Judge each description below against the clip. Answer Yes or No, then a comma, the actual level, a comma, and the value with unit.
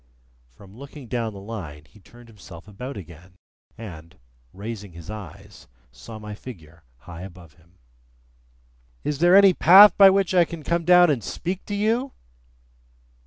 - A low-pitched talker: Yes, low, 110 Hz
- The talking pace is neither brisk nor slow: Yes, average, 155 wpm